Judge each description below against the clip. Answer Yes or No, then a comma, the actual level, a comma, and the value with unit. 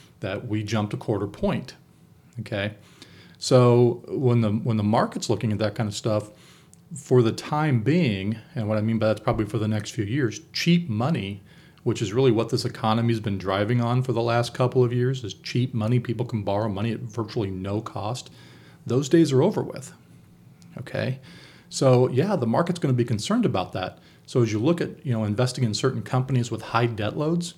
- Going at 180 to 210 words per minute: Yes, average, 200 wpm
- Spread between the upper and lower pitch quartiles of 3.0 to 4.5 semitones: Yes, average, 3.3 semitones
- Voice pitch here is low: Yes, low, 120 Hz